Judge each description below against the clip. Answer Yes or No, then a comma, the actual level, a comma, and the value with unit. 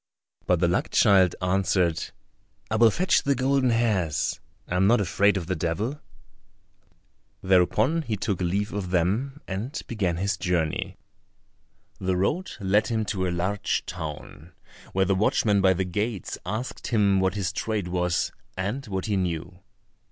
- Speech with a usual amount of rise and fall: Yes, average, 3.2 semitones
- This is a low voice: Yes, very low, 95 Hz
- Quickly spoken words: No, average, 155 wpm